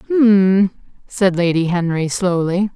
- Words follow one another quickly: No, slow, 110 wpm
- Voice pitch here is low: No, high, 190 Hz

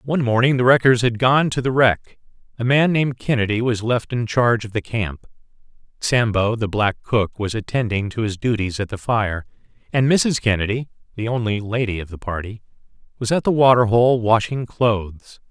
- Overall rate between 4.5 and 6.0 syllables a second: Yes, 5.2 syllables/s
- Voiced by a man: Yes, male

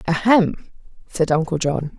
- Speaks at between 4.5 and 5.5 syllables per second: No, 4.1 syllables/s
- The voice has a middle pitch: Yes, medium, 175 Hz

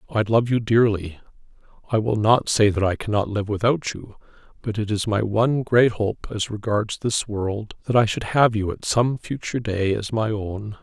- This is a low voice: Yes, low, 110 Hz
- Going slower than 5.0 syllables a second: Yes, 4.8 syllables/s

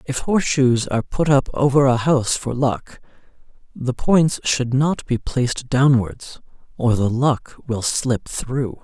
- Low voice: Yes, low, 130 Hz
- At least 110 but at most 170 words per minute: Yes, average, 155 wpm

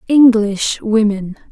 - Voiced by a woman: Yes, female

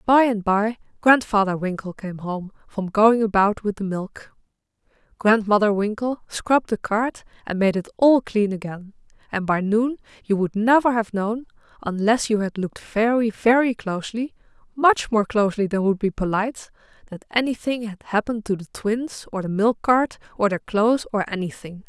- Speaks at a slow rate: No, average, 165 wpm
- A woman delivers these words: Yes, female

